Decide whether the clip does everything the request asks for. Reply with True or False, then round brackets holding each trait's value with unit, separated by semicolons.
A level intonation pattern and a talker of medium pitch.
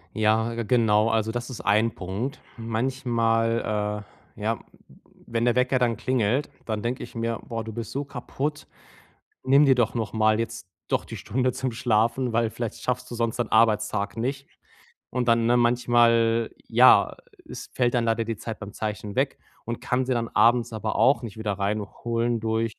False (1.8 semitones; 115 Hz)